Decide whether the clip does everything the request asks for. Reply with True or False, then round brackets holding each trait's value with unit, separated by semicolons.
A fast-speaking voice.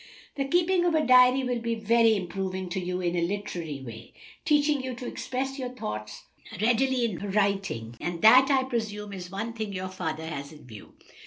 False (190 wpm)